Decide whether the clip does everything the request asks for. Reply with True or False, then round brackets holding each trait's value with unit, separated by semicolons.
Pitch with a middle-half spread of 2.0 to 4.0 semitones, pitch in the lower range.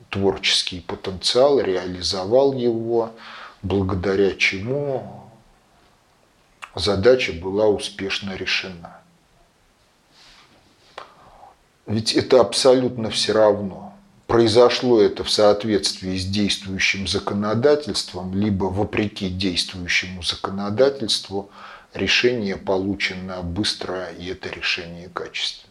True (2.8 semitones; 100 Hz)